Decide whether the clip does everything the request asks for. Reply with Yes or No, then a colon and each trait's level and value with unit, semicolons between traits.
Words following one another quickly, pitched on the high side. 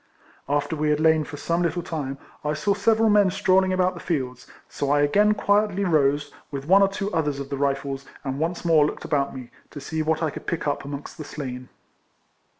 No: fast, 215 wpm; medium, 155 Hz